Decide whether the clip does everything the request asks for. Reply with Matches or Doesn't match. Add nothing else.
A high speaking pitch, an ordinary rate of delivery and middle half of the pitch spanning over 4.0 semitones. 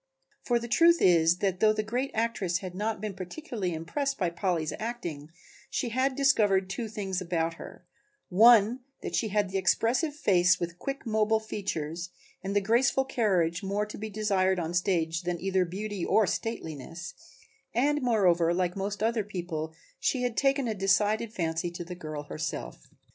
Matches